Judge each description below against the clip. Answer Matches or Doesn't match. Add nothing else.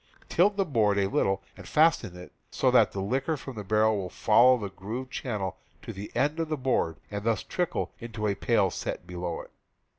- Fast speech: Matches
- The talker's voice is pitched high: Doesn't match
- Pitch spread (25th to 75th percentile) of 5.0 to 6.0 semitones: Matches